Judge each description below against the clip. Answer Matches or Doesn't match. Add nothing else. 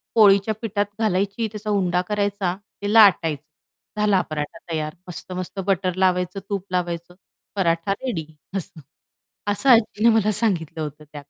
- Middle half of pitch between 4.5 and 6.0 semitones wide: Doesn't match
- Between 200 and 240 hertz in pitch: Doesn't match